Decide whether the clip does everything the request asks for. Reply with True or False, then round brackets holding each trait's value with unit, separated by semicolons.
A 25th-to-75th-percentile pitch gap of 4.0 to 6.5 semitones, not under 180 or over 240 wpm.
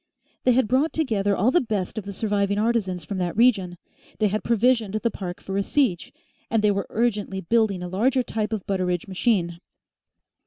False (3.5 semitones; 190 wpm)